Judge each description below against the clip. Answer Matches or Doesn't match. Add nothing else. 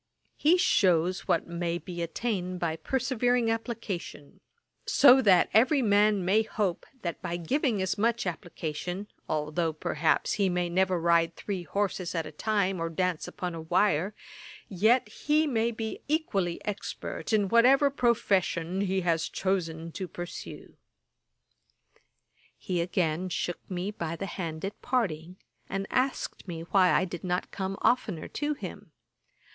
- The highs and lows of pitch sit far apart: Doesn't match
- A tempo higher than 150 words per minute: Doesn't match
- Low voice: Doesn't match